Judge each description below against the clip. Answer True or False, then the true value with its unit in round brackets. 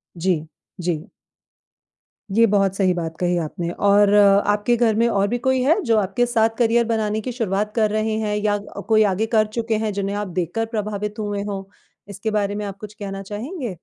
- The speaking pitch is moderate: False (210 Hz)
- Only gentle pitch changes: True (2.1 semitones)